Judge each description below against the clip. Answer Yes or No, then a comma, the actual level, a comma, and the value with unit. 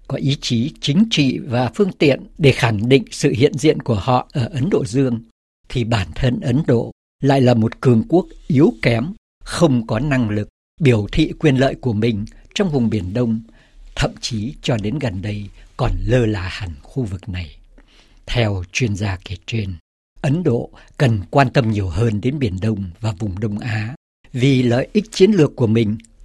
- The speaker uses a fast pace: No, average, 195 wpm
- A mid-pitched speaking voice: No, low, 120 Hz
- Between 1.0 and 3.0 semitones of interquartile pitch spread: No, average, 4.4 semitones